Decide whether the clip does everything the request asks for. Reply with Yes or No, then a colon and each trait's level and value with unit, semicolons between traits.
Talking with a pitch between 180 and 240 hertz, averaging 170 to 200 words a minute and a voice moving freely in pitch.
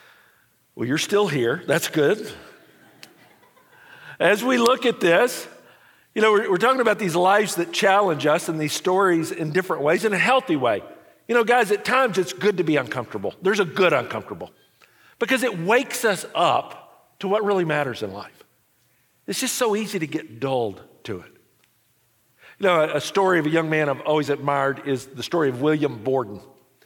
Yes: medium, 185 Hz; average, 190 wpm; wide, 6.8 semitones